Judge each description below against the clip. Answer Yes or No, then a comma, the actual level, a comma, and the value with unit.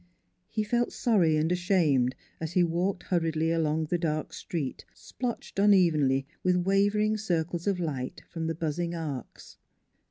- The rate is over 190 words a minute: No, average, 145 wpm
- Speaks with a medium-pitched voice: Yes, medium, 170 Hz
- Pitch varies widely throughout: No, average, 3.5 semitones